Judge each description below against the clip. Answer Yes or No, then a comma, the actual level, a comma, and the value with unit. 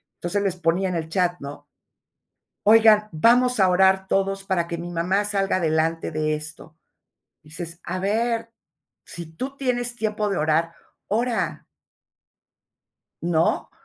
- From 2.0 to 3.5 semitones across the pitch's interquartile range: No, average, 4.3 semitones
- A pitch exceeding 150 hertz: Yes, medium, 185 Hz